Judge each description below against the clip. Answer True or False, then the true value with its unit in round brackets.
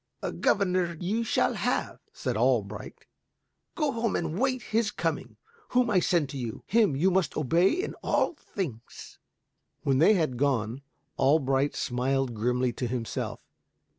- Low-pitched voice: False (160 Hz)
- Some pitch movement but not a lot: False (7.7 semitones)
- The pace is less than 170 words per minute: True (145 wpm)